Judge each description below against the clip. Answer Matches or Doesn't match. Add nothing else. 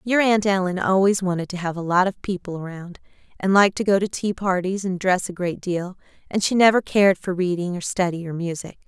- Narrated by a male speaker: Doesn't match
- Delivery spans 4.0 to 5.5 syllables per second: Doesn't match